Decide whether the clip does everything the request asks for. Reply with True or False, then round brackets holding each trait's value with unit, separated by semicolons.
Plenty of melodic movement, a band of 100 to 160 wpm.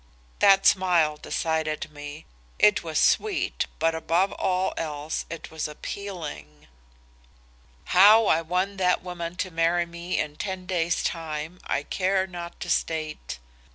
False (3.0 semitones; 135 wpm)